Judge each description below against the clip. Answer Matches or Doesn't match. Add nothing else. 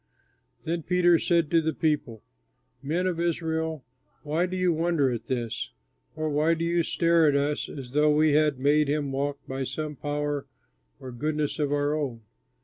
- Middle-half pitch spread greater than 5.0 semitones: Doesn't match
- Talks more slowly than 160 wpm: Doesn't match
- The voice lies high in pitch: Doesn't match